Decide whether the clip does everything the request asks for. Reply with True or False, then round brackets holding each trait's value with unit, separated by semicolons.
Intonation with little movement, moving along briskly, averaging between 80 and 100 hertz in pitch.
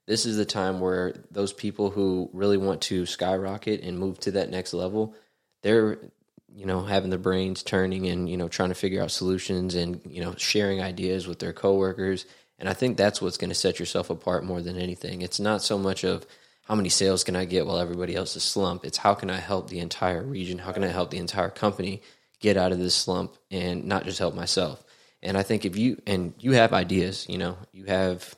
True (1.6 semitones; 230 wpm; 95 Hz)